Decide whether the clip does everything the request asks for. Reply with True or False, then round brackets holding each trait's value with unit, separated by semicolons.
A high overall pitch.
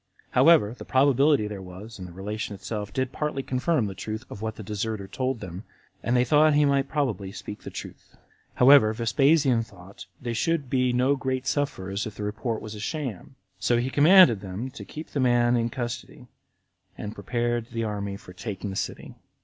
False (120 Hz)